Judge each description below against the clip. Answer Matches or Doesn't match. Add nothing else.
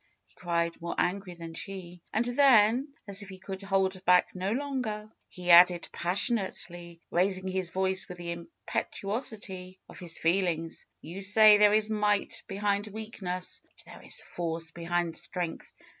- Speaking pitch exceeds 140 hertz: Matches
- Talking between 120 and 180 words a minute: Matches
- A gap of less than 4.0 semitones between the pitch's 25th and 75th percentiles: Matches